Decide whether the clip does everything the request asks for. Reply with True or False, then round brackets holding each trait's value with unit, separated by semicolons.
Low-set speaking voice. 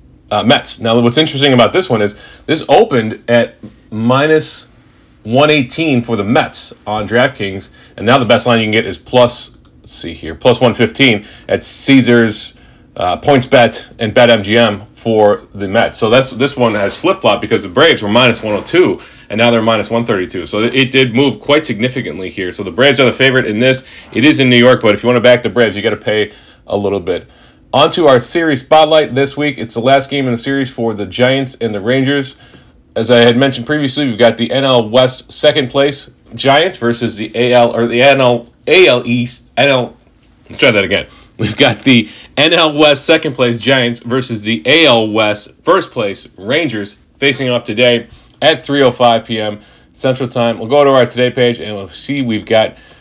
True (120 Hz)